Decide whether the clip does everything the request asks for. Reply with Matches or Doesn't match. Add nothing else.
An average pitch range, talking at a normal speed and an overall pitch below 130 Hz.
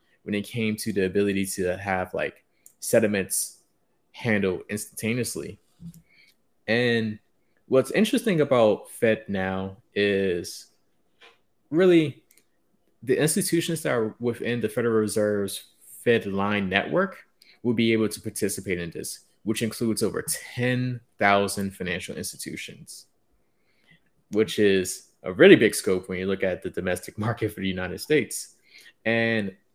Doesn't match